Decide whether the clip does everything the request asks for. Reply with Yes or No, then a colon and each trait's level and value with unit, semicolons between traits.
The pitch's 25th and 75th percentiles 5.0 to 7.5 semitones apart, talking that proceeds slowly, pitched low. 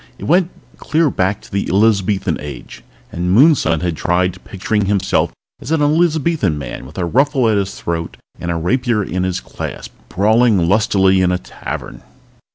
No: wide, 5.5 semitones; average, 165 wpm; low, 100 Hz